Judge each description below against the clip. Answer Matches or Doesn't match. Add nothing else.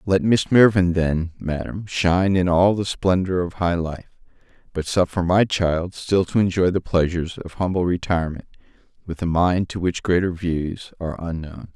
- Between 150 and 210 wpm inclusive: Matches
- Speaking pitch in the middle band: Doesn't match